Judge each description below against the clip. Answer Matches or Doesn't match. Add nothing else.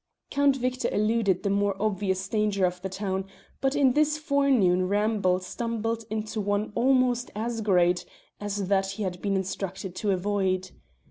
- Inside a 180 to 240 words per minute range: Doesn't match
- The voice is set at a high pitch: Matches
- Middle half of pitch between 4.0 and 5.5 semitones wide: Doesn't match